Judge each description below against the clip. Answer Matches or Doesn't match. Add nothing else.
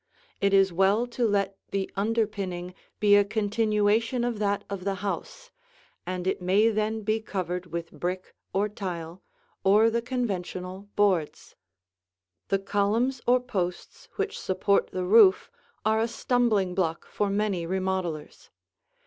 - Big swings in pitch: Doesn't match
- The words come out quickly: Doesn't match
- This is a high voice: Matches